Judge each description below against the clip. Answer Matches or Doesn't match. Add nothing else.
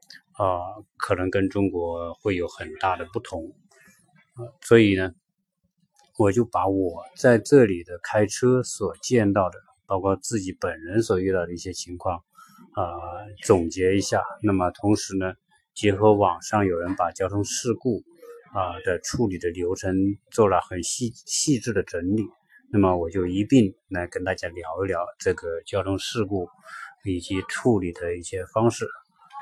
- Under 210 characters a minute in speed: Doesn't match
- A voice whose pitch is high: Doesn't match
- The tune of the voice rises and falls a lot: Doesn't match